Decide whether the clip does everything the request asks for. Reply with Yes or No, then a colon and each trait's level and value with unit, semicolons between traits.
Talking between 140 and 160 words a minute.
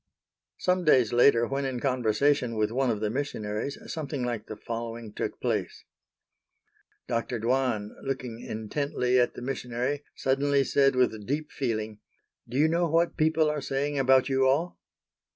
Yes: average, 150 wpm